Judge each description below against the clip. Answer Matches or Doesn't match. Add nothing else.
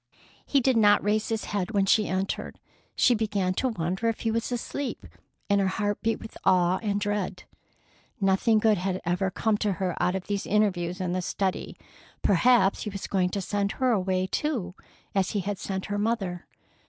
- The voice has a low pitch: Doesn't match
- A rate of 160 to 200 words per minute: Matches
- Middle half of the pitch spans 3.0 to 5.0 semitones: Doesn't match